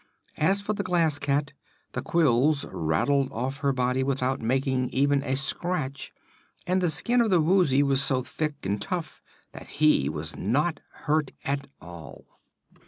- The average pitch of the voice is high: No, medium, 140 Hz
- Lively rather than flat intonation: No, average, 3.4 semitones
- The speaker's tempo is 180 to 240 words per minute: No, average, 160 wpm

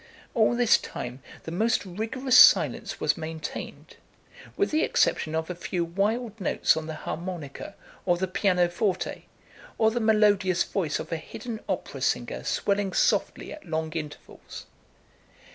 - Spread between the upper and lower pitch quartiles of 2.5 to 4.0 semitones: No, average, 5.2 semitones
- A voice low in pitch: No, medium, 185 Hz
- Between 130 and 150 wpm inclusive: Yes, average, 145 wpm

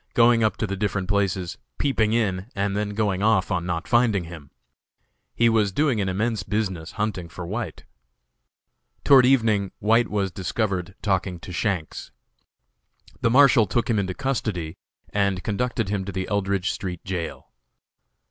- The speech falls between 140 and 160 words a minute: Yes, average, 155 wpm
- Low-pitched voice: Yes, low, 100 Hz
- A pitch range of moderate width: Yes, average, 3.1 semitones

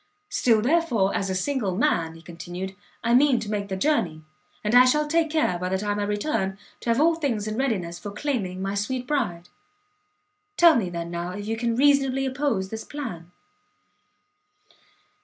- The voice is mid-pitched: No, high, 215 Hz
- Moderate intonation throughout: No, wide, 6.2 semitones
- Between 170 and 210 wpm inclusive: Yes, average, 180 wpm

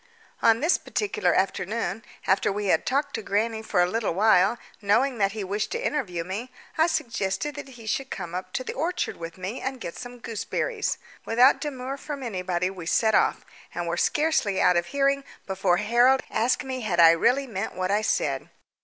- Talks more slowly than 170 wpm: No, average, 190 wpm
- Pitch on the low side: No, high, 220 Hz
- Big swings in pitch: Yes, wide, 5.9 semitones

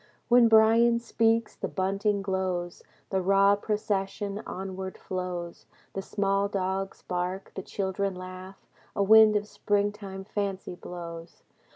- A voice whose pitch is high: Yes, high, 195 Hz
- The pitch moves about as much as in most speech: No, narrow, 1.8 semitones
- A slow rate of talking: Yes, slow, 125 wpm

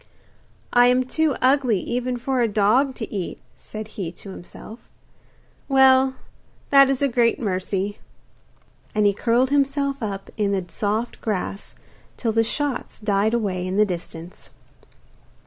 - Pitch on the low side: No, high, 225 Hz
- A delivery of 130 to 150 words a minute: Yes, average, 145 wpm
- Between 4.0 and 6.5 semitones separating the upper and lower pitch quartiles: Yes, average, 4.5 semitones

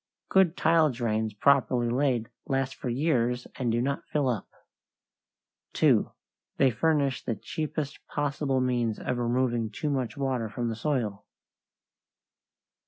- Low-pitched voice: Yes, low, 130 Hz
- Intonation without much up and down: No, average, 3.1 semitones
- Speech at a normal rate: No, slow, 130 wpm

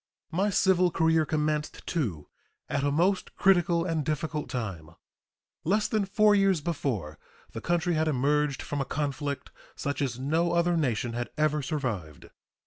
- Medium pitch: Yes, medium, 150 Hz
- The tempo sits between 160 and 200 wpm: No, average, 150 wpm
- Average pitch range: Yes, average, 4.2 semitones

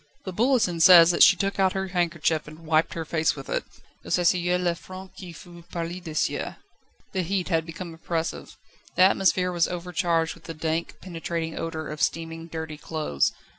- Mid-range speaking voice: Yes, medium, 170 Hz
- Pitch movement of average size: No, narrow, 2.0 semitones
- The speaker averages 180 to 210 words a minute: Yes, average, 185 wpm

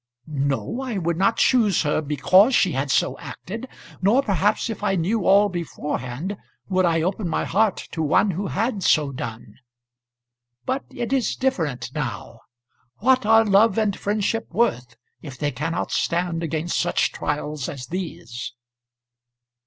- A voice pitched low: No, medium, 180 Hz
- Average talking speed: Yes, average, 150 wpm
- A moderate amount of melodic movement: No, wide, 6.1 semitones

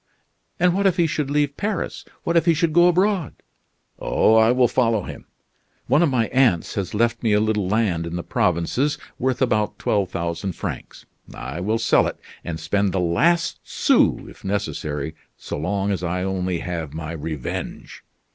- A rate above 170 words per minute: Yes, average, 180 wpm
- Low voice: Yes, low, 105 Hz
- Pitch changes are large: Yes, wide, 8.4 semitones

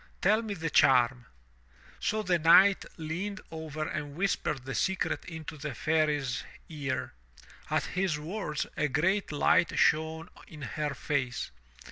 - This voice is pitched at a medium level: Yes, medium, 155 Hz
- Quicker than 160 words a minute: No, slow, 135 wpm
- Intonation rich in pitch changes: No, average, 3.7 semitones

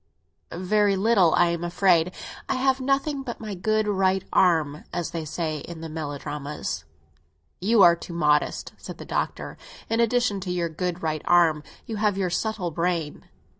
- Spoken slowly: No, average, 170 wpm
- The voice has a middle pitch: Yes, medium, 180 Hz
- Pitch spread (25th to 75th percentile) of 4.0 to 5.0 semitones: Yes, average, 4.5 semitones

